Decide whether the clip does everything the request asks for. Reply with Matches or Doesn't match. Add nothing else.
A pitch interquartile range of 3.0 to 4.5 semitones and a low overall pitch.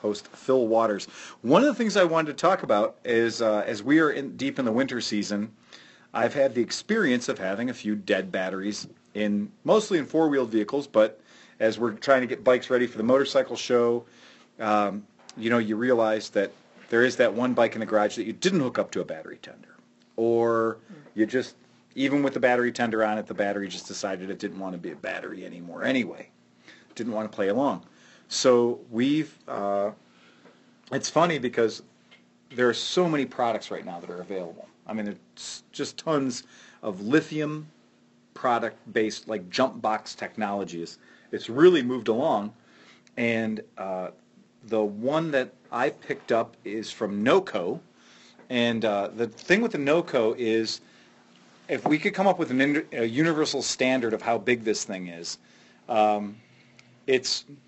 Matches